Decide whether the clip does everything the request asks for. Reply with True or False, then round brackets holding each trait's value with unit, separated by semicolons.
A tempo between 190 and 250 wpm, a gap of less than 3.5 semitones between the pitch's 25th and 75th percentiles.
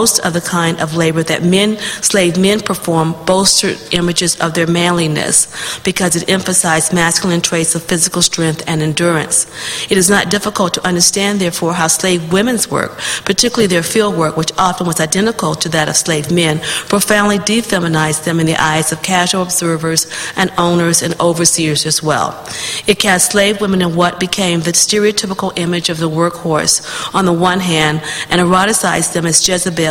False (175 wpm; 2.6 semitones)